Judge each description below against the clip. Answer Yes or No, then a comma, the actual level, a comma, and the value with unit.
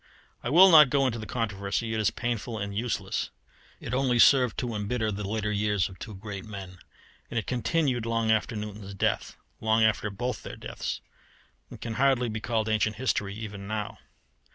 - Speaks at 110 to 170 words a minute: No, average, 185 wpm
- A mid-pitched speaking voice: No, low, 110 Hz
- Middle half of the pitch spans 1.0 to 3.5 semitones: Yes, average, 2.7 semitones